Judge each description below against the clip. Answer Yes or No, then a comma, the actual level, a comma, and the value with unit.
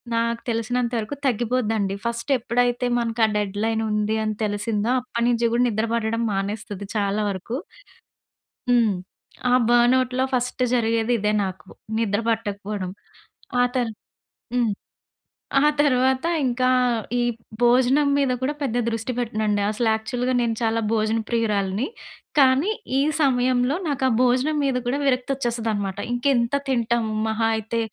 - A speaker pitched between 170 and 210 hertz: No, high, 235 Hz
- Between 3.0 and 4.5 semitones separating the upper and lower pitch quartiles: No, narrow, 2.5 semitones